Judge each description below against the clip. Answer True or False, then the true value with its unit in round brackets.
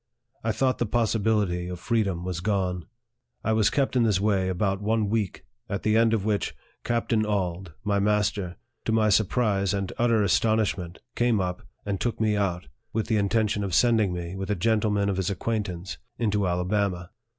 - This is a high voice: False (105 Hz)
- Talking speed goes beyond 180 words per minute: True (190 wpm)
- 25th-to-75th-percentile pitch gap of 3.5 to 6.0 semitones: False (3.0 semitones)